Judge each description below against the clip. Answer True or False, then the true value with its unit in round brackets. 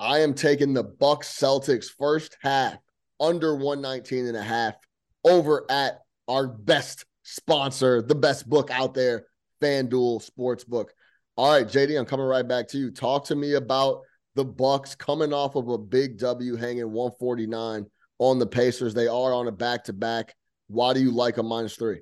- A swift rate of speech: False (170 wpm)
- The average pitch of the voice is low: True (130 Hz)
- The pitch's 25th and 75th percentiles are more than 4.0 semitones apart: False (2.8 semitones)